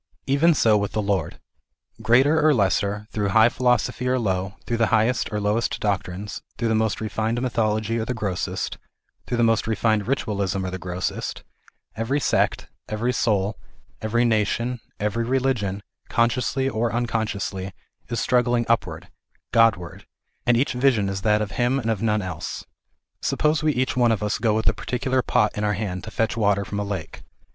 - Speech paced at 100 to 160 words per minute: No, average, 185 wpm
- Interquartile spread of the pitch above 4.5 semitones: No, average, 2.9 semitones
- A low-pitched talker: Yes, low, 110 Hz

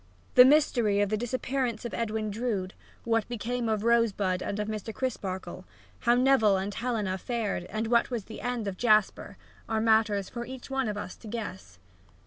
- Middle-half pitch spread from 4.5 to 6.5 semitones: No, average, 2.8 semitones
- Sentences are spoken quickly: No, average, 180 wpm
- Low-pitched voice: No, high, 220 Hz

